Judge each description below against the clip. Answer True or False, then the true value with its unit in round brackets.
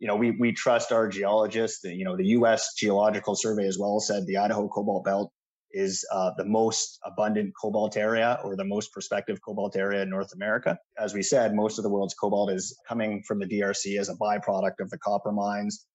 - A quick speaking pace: True (215 wpm)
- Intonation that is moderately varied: False (1.6 semitones)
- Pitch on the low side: True (105 Hz)